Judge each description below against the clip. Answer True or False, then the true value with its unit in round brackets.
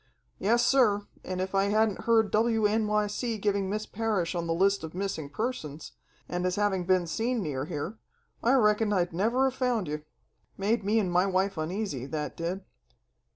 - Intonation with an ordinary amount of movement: True (3.7 semitones)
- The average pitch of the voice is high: True (200 Hz)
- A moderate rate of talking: True (170 wpm)